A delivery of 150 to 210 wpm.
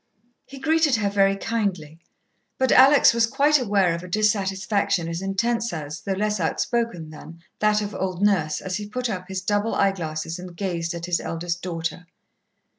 Yes: average, 180 wpm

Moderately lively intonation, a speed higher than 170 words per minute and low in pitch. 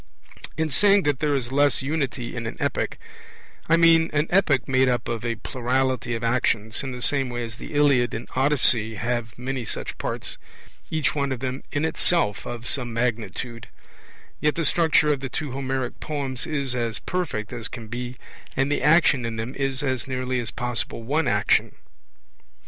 Yes: average, 3.4 semitones; average, 185 wpm; low, 130 Hz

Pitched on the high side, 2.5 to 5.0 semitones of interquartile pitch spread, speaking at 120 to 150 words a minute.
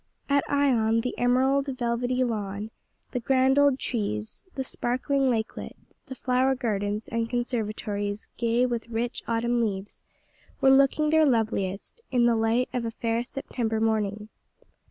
Yes: high, 235 Hz; average, 2.8 semitones; average, 140 wpm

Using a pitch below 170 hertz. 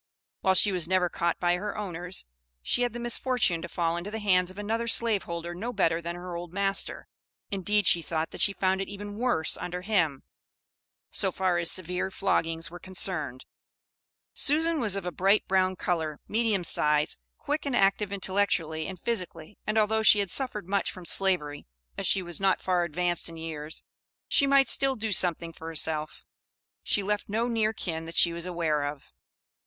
No: medium, 185 Hz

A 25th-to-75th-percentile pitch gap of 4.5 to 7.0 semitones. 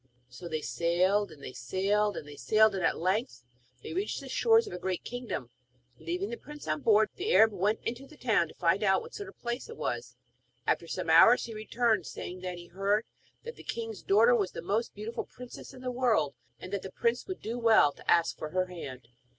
Yes: average, 5.1 semitones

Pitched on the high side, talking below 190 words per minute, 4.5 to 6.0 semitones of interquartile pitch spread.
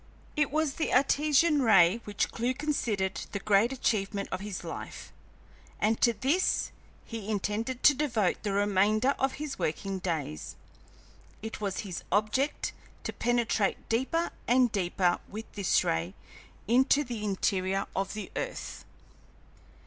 Yes: high, 215 Hz; slow, 135 wpm; average, 5.0 semitones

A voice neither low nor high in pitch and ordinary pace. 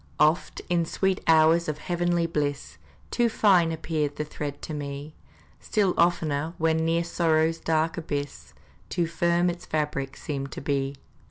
Yes: medium, 160 Hz; average, 150 wpm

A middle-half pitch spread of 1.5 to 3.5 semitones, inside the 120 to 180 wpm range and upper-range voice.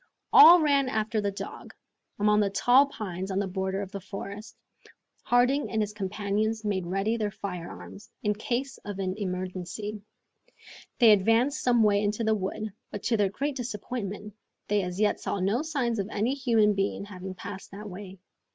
Yes: average, 2.7 semitones; average, 175 wpm; high, 210 Hz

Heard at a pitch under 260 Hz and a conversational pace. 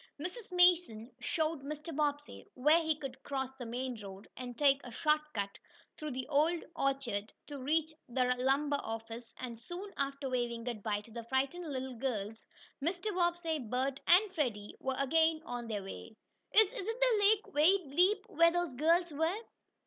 No: very high, 280 Hz; average, 170 wpm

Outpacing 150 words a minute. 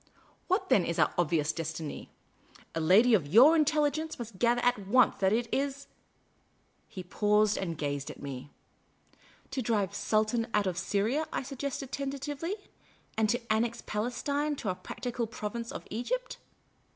Yes: average, 170 wpm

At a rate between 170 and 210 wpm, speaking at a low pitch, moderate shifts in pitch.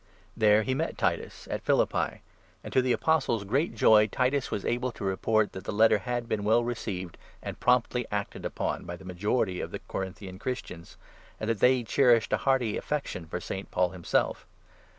Yes: average, 185 wpm; low, 110 Hz; average, 4.5 semitones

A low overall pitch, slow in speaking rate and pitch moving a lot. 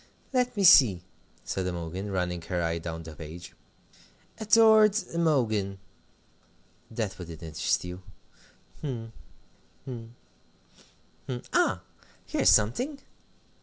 Yes: low, 100 Hz; slow, 100 wpm; wide, 8.9 semitones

